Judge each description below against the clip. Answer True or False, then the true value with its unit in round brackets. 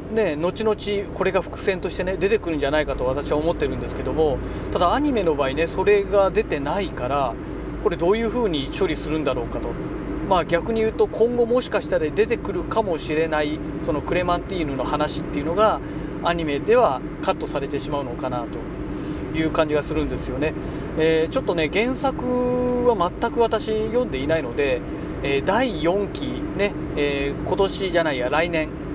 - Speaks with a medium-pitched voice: True (170 Hz)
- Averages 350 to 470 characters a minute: True (370 characters per minute)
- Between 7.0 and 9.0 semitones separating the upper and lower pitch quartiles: False (6.0 semitones)